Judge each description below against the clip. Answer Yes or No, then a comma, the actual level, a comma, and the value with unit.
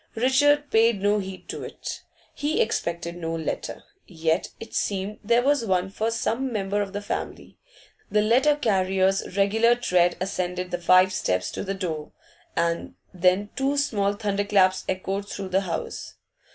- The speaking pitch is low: No, high, 195 Hz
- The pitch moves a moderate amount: Yes, average, 3.6 semitones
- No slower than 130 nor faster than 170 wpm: Yes, average, 155 wpm